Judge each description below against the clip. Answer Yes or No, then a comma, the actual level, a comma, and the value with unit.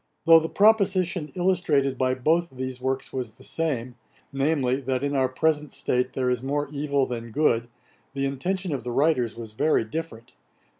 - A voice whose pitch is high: No, low, 135 Hz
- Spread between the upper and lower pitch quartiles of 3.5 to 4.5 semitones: Yes, average, 4.1 semitones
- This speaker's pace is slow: No, average, 170 wpm